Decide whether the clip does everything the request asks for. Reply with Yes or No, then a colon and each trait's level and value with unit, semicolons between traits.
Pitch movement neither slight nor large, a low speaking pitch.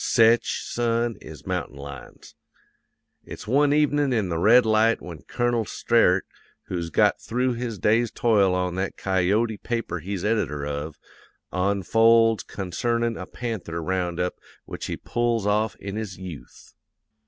Yes: average, 4.5 semitones; low, 105 Hz